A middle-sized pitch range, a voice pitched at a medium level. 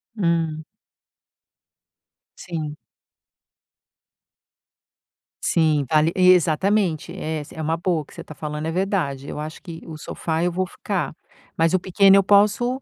Yes: average, 3.3 semitones; medium, 165 Hz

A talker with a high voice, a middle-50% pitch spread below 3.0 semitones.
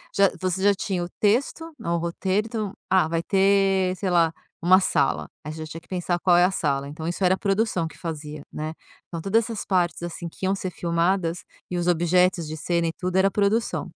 No: medium, 180 Hz; narrow, 2.6 semitones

